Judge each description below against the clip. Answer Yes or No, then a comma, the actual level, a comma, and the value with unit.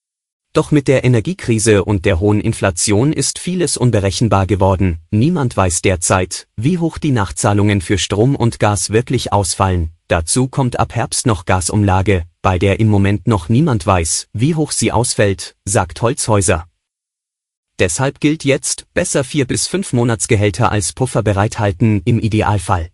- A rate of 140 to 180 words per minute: Yes, average, 150 wpm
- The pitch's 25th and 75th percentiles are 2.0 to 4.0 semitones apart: No, average, 4.5 semitones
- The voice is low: Yes, low, 110 Hz